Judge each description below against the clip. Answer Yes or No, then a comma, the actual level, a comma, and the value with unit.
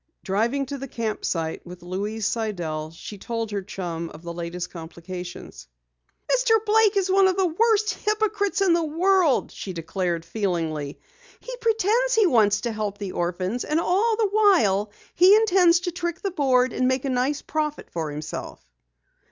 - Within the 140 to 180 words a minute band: Yes, average, 170 wpm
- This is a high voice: Yes, very high, 250 Hz